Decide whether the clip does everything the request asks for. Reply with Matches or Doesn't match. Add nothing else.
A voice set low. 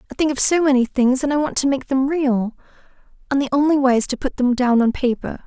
Doesn't match